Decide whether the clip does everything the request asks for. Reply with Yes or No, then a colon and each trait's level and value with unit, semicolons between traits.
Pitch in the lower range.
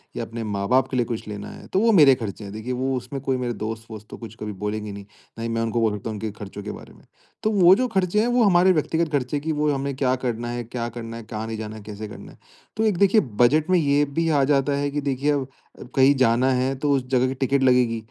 Yes: low, 125 Hz